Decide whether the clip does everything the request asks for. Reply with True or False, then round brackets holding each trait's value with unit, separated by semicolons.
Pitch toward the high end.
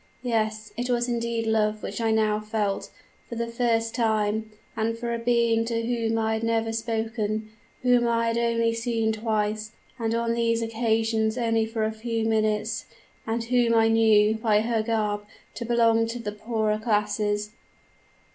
True (225 Hz)